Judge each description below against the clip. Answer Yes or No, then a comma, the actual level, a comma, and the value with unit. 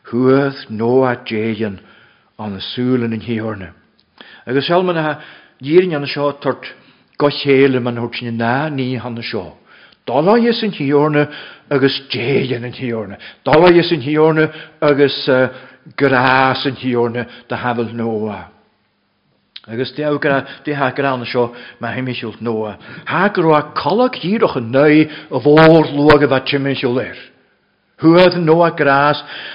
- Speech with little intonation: No, average, 3.7 semitones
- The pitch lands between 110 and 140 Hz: Yes, low, 135 Hz